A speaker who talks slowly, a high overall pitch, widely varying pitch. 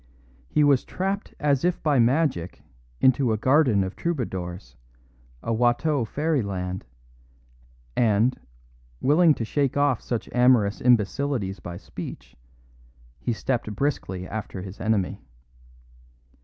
No: slow, 115 wpm; low, 120 Hz; wide, 6.1 semitones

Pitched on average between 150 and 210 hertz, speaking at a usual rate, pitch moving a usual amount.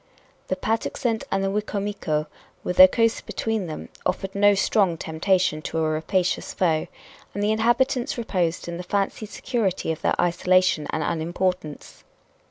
Yes: medium, 185 Hz; average, 150 wpm; average, 4.0 semitones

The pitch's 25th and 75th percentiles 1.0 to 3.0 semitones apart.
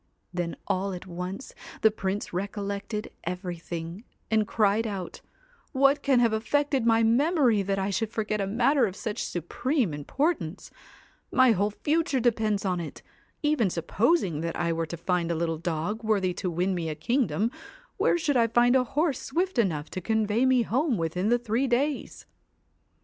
No: wide, 5.4 semitones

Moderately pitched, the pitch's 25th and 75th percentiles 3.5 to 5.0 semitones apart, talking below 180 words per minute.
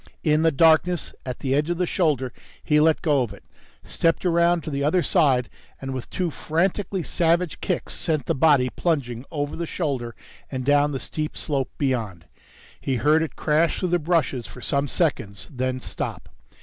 No: medium, 150 Hz; average, 4.1 semitones; average, 185 wpm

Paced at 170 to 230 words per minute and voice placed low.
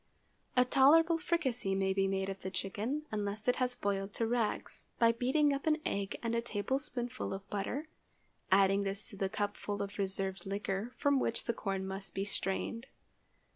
No: average, 175 wpm; high, 205 Hz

